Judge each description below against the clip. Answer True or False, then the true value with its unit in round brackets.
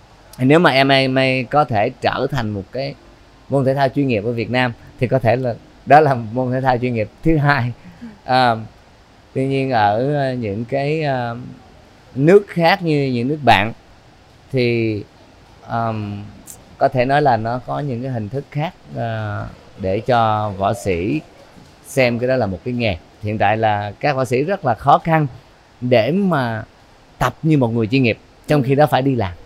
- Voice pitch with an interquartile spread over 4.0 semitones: False (3.6 semitones)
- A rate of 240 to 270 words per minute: False (180 wpm)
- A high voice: False (125 Hz)